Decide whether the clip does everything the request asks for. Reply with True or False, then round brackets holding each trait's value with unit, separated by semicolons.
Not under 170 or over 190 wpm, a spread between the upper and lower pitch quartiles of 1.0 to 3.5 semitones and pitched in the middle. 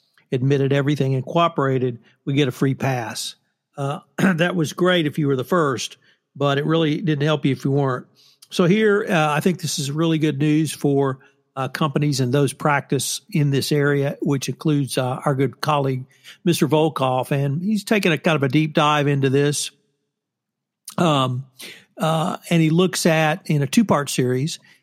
True (185 wpm; 2.8 semitones; 145 Hz)